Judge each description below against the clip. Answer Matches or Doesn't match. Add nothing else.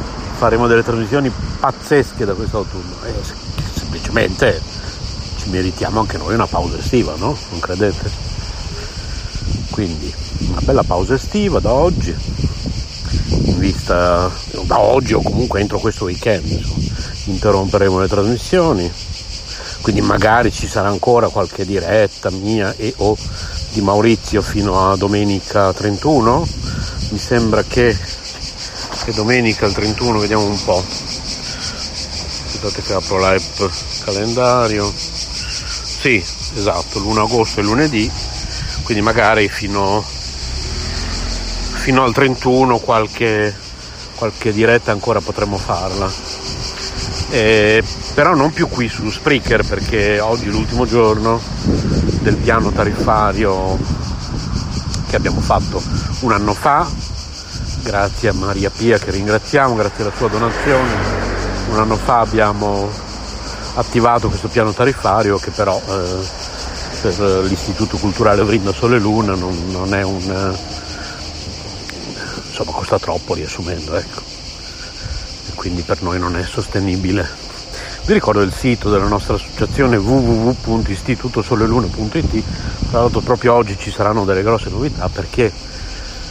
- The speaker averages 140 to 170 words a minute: Doesn't match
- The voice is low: Matches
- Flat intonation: Doesn't match